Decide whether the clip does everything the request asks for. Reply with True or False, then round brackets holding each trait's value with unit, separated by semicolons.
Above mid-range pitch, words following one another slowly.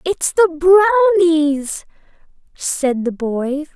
True (320 Hz; 95 wpm)